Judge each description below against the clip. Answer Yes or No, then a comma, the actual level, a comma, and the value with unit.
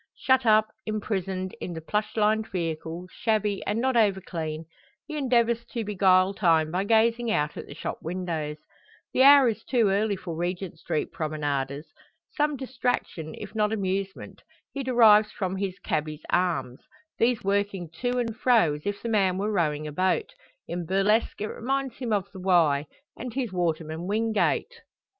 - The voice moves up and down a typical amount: Yes, average, 5.0 semitones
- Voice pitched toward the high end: Yes, high, 200 Hz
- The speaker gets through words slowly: No, average, 165 wpm